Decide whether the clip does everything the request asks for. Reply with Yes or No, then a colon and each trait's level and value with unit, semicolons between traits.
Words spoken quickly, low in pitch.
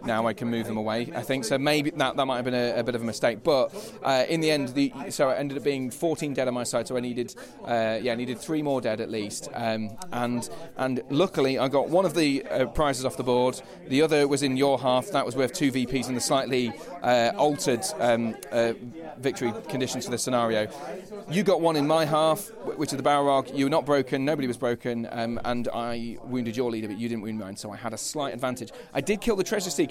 Yes: fast, 255 wpm; low, 130 Hz